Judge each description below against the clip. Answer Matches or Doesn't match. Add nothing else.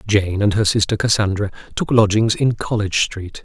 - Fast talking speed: Doesn't match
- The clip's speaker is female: Doesn't match